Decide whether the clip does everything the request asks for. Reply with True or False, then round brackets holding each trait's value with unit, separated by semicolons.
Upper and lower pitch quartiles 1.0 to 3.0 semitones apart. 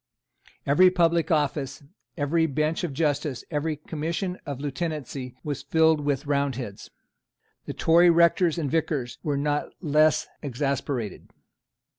True (2.6 semitones)